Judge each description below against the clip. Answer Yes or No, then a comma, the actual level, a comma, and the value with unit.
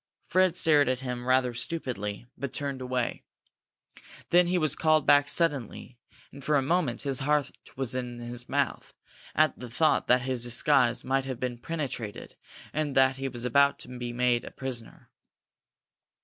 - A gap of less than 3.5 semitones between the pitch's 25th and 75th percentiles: Yes, average, 2.8 semitones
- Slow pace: No, average, 165 wpm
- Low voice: Yes, low, 130 Hz